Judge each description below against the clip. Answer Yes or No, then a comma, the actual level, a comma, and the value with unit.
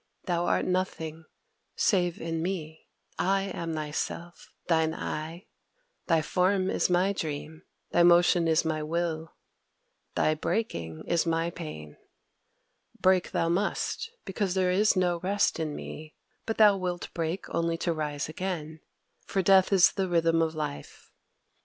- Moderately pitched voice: Yes, medium, 170 Hz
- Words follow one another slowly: No, average, 145 wpm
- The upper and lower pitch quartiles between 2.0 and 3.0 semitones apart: Yes, average, 2.7 semitones